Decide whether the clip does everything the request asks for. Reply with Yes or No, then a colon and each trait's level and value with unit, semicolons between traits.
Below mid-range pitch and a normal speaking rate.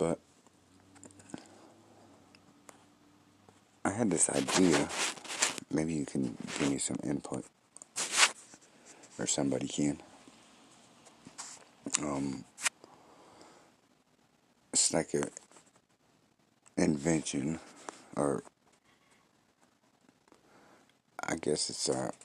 No: very low, 80 Hz; slow, 65 wpm